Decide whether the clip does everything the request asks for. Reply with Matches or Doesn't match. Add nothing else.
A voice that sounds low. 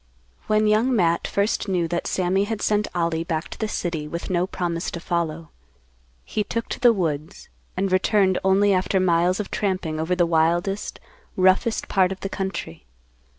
Doesn't match